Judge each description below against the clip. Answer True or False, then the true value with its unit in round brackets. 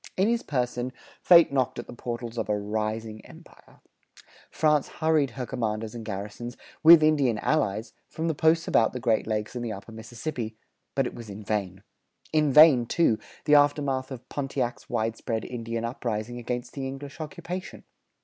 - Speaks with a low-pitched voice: True (120 Hz)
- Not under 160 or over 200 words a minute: True (170 wpm)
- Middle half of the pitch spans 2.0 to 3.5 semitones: False (4.7 semitones)